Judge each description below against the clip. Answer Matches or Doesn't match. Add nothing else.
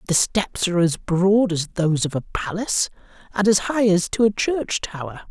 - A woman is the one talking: Doesn't match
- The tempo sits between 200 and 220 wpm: Matches